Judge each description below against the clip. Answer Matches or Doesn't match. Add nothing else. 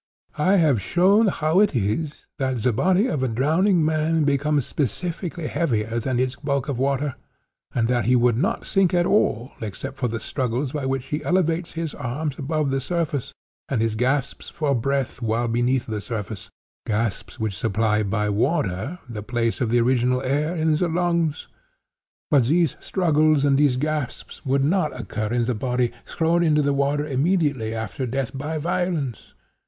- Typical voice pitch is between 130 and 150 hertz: Matches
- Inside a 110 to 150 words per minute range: Doesn't match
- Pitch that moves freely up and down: Doesn't match